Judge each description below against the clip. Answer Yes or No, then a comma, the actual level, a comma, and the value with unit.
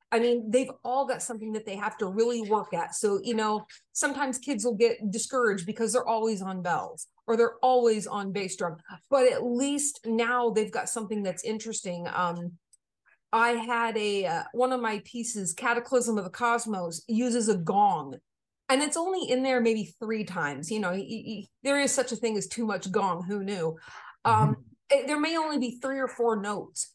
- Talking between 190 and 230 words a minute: Yes, average, 200 wpm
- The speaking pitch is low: No, high, 225 Hz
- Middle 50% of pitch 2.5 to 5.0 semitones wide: Yes, average, 3.5 semitones